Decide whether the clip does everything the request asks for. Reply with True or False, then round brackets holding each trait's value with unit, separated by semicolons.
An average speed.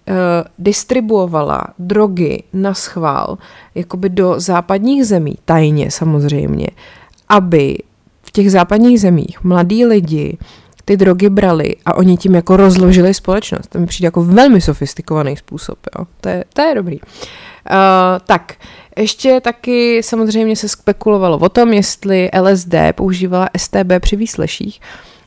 True (130 wpm)